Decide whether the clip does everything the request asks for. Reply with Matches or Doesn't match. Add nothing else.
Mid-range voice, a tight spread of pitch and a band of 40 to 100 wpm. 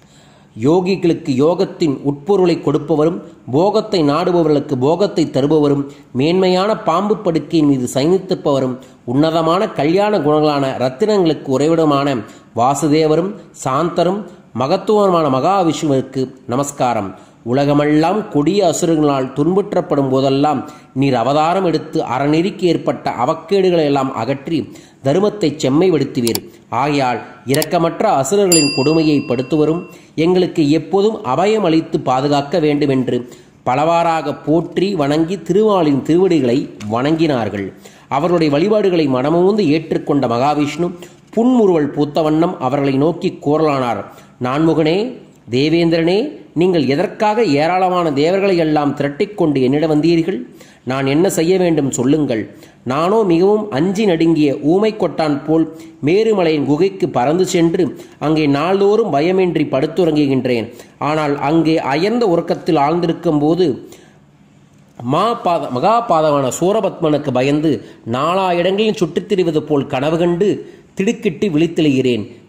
Doesn't match